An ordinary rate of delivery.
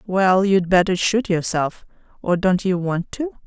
Yes: average, 175 wpm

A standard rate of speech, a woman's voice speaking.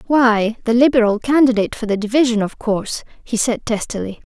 Yes: average, 165 wpm; female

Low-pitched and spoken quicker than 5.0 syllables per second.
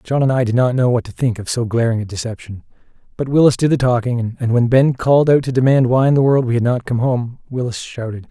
Yes: low, 125 Hz; 6.1 syllables/s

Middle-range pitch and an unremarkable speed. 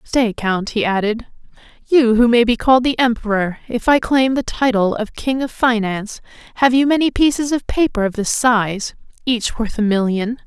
No: high, 235 Hz; average, 190 wpm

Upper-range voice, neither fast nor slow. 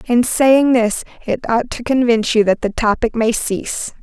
Yes: high, 235 Hz; average, 195 wpm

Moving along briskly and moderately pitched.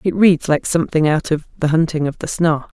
Yes: fast, 235 wpm; medium, 160 Hz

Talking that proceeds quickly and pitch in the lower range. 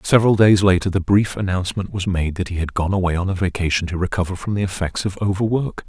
Yes: fast, 235 wpm; very low, 95 Hz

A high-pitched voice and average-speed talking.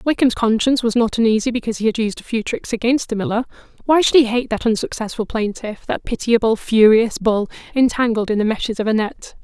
No: high, 225 Hz; fast, 210 wpm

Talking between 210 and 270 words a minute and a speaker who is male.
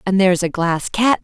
No: fast, 240 wpm; female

